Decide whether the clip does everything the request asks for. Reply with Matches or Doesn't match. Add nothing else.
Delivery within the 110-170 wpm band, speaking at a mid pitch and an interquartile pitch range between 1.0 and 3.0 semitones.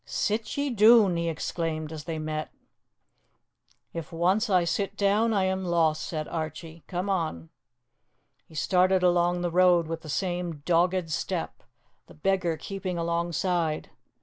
Matches